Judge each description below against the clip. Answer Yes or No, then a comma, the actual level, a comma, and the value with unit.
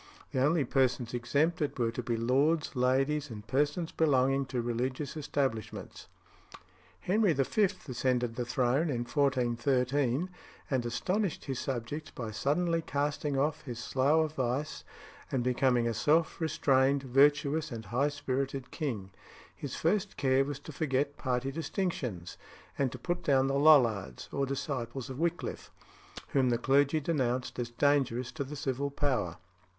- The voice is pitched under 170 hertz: Yes, low, 135 Hz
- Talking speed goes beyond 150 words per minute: No, average, 145 wpm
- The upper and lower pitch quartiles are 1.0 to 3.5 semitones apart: Yes, average, 3.1 semitones